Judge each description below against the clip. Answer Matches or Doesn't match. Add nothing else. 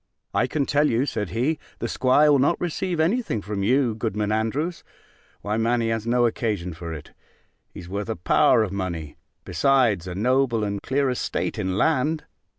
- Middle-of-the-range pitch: Doesn't match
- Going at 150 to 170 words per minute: Doesn't match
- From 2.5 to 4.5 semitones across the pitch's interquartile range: Doesn't match